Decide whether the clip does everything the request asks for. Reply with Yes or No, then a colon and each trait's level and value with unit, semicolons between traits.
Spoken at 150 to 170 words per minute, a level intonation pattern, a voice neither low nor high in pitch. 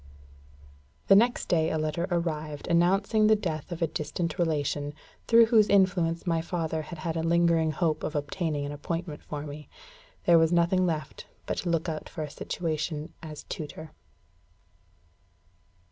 Yes: average, 160 wpm; narrow, 2.3 semitones; medium, 165 Hz